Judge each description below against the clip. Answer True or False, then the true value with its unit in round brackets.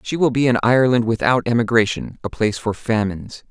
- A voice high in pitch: False (115 Hz)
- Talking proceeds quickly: False (190 wpm)